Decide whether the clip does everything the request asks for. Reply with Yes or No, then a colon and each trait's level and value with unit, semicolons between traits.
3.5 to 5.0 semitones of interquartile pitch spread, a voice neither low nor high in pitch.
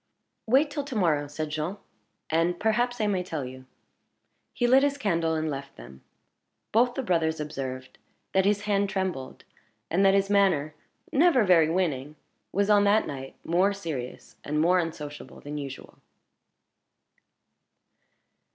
No: wide, 5.5 semitones; medium, 175 Hz